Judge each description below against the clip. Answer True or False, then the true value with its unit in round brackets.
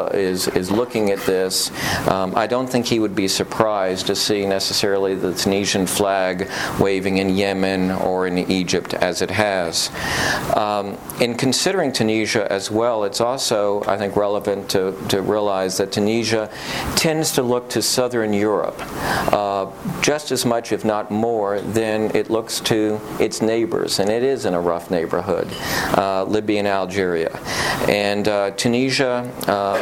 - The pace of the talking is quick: False (155 wpm)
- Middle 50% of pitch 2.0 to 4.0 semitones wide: True (2.8 semitones)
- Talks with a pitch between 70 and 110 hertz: True (100 Hz)